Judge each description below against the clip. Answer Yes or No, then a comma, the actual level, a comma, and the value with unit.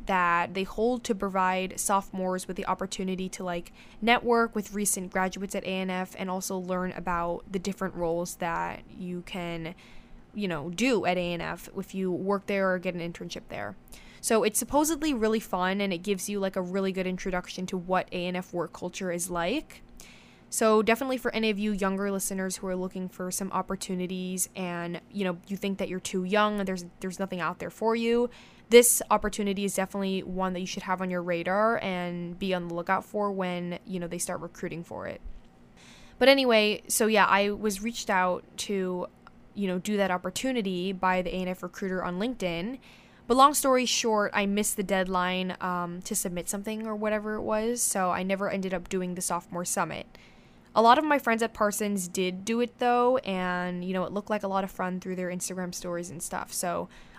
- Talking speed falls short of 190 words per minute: No, average, 200 wpm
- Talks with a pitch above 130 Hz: Yes, high, 190 Hz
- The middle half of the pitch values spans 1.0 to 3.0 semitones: Yes, narrow, 2.6 semitones